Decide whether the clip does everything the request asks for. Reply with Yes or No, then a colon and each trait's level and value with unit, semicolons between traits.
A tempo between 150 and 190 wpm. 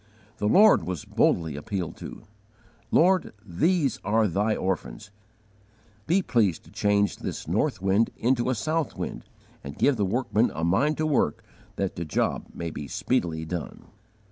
Yes: average, 155 wpm